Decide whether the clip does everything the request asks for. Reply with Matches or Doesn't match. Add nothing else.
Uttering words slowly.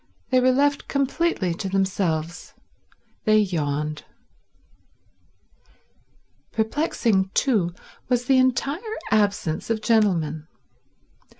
Matches